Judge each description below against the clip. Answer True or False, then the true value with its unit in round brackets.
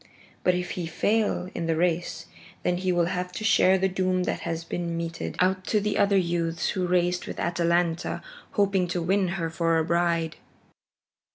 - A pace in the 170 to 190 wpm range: True (185 wpm)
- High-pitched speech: False (175 Hz)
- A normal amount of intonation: False (1.7 semitones)